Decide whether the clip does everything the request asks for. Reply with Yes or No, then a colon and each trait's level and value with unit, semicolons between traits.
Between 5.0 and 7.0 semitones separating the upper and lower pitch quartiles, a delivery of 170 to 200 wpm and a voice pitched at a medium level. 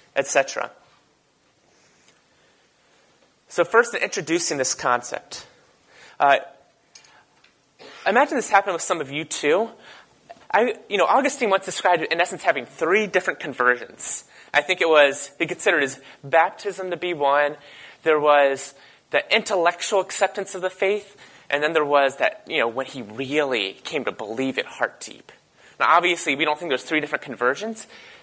No: average, 5.3 semitones; average, 155 wpm; medium, 165 Hz